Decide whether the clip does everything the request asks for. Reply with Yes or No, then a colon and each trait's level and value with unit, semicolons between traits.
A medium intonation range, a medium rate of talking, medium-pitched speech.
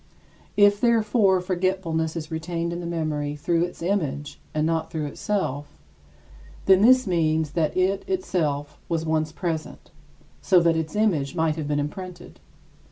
Yes: average, 3.4 semitones; average, 150 wpm; medium, 165 Hz